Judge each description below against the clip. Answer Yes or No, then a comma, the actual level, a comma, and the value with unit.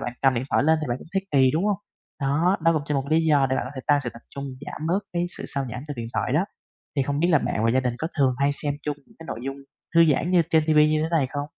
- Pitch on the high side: No, medium, 145 Hz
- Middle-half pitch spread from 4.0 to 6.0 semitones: No, average, 3.3 semitones